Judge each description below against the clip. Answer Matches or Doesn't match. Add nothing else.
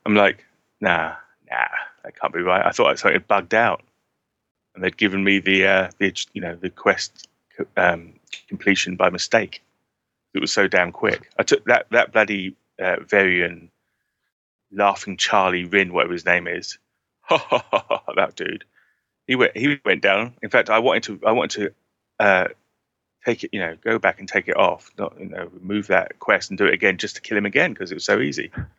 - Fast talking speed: Doesn't match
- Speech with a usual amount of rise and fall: Doesn't match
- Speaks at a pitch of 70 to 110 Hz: Matches